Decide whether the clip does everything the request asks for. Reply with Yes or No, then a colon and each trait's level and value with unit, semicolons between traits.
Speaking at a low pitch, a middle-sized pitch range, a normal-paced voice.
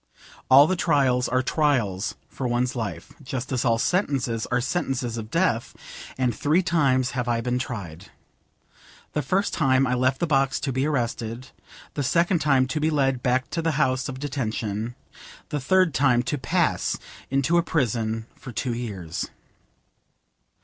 Yes: low, 130 Hz; average, 3.5 semitones; average, 160 wpm